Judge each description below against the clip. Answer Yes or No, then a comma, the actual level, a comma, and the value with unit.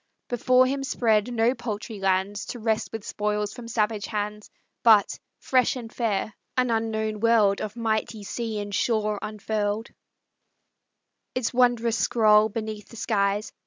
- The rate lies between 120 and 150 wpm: Yes, average, 140 wpm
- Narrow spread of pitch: Yes, narrow, 1.9 semitones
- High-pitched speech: Yes, high, 220 Hz